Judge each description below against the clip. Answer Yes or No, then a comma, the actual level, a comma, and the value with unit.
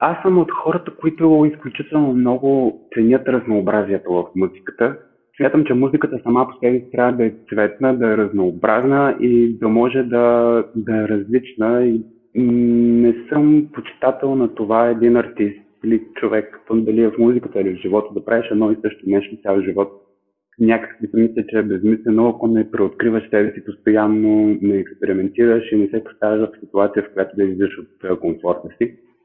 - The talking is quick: Yes, fast, 175 wpm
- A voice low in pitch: Yes, low, 115 Hz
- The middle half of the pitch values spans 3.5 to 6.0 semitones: No, average, 2.7 semitones